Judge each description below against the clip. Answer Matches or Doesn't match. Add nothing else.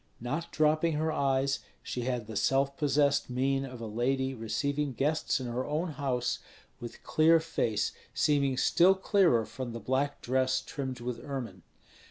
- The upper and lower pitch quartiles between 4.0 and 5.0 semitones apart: Doesn't match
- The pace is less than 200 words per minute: Matches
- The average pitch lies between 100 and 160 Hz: Matches